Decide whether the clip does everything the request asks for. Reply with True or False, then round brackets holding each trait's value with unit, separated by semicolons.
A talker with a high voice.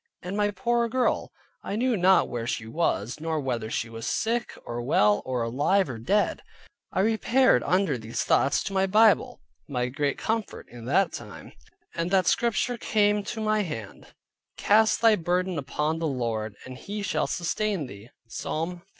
False (170 Hz)